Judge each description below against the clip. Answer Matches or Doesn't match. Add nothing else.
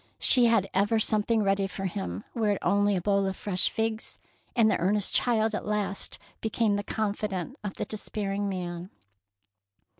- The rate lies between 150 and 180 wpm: Matches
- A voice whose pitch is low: Doesn't match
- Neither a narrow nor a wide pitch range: Doesn't match